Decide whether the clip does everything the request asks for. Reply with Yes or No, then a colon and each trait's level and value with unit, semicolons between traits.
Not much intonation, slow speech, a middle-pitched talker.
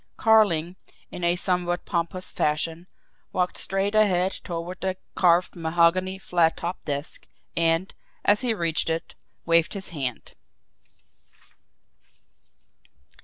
Yes: narrow, 2.1 semitones; slow, 110 wpm; medium, 175 Hz